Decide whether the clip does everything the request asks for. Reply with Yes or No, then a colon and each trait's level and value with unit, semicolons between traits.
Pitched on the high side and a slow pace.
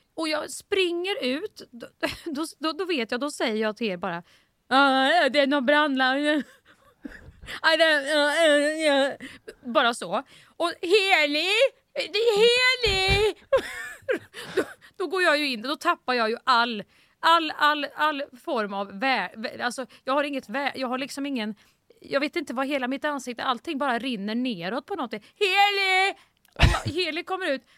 No: very high, 290 Hz; average, 145 wpm